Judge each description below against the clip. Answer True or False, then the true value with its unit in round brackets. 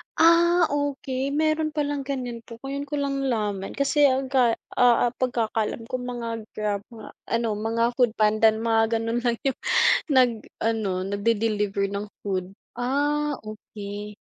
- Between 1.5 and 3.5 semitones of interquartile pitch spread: False (4.1 semitones)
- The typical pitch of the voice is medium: False (235 Hz)